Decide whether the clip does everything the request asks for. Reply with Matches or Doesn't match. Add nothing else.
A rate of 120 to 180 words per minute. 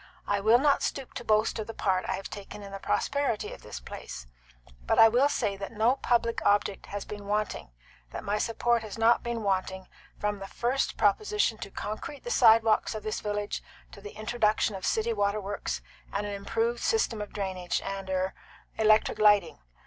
Doesn't match